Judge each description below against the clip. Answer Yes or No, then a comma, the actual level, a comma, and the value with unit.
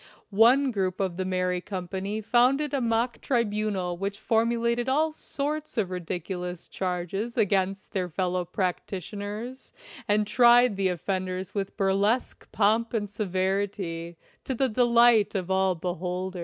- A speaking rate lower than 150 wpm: Yes, slow, 135 wpm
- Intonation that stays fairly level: No, average, 4.1 semitones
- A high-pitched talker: Yes, high, 200 Hz